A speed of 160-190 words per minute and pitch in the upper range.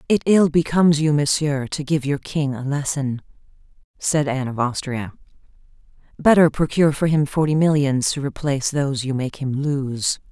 No: average, 165 wpm; medium, 145 Hz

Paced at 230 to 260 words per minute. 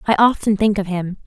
Yes: fast, 235 wpm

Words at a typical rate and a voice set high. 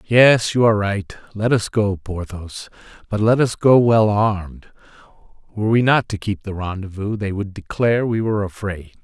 No: average, 180 wpm; low, 105 Hz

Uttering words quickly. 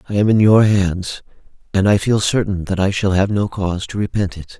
Yes: fast, 235 wpm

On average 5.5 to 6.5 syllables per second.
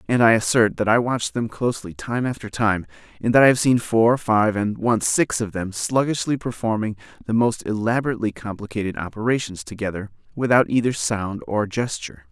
Yes: 5.7 syllables/s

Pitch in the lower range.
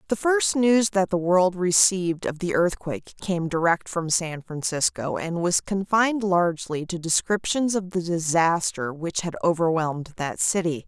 No: medium, 175 Hz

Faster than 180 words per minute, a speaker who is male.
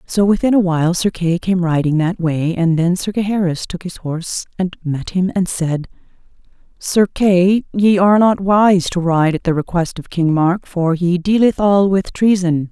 No: average, 200 wpm; female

